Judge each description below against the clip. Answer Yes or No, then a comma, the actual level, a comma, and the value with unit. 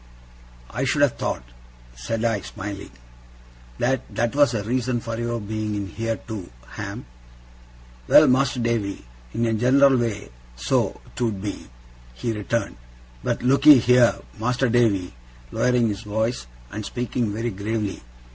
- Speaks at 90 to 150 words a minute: Yes, average, 145 wpm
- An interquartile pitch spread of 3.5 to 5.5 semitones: No, average, 3.0 semitones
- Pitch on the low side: Yes, low, 115 Hz